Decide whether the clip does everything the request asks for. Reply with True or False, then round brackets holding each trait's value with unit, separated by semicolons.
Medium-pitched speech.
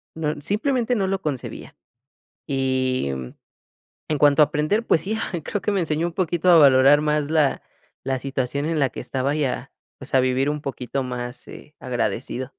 True (145 Hz)